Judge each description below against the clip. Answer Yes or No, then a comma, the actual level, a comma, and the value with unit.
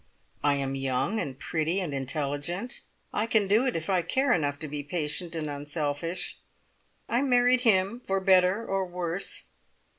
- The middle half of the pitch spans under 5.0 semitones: No, wide, 5.4 semitones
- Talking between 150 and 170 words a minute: Yes, average, 160 wpm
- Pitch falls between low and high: Yes, medium, 175 Hz